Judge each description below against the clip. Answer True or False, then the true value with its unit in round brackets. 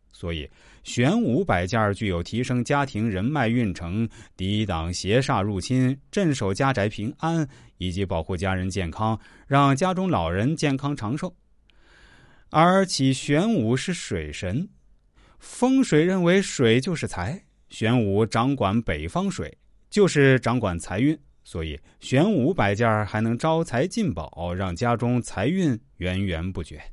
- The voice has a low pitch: True (115 Hz)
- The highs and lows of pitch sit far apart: True (6.9 semitones)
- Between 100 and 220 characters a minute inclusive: True (210 characters per minute)